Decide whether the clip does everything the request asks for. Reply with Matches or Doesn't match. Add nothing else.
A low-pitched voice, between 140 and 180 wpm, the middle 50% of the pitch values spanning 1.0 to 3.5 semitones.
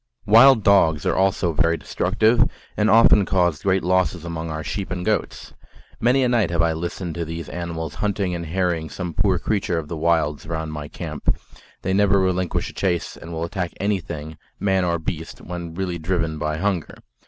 Doesn't match